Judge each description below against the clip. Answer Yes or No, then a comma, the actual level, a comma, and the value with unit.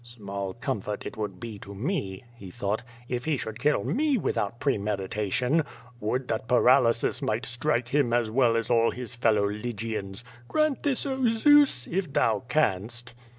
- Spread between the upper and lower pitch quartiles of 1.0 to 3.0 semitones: No, average, 4.6 semitones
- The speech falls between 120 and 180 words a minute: Yes, average, 160 wpm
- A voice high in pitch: No, low, 120 Hz